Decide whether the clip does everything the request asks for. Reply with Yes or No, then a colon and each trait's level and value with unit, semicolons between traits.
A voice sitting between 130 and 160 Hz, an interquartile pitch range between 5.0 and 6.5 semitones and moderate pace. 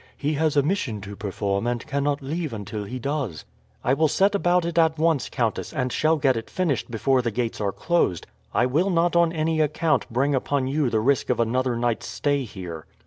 No: low, 135 Hz; average, 5.3 semitones; fast, 210 wpm